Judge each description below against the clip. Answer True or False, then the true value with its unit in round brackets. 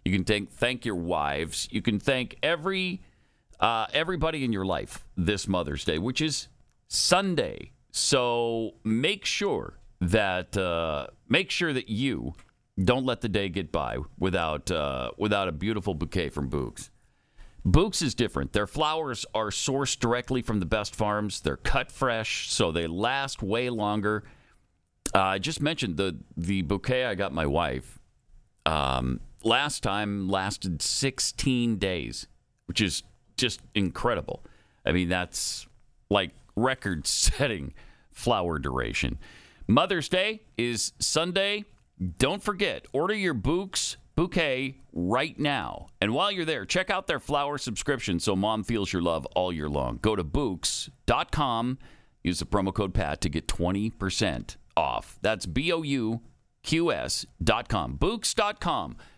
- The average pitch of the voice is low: True (105 Hz)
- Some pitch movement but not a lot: False (5.9 semitones)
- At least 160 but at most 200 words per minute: False (145 wpm)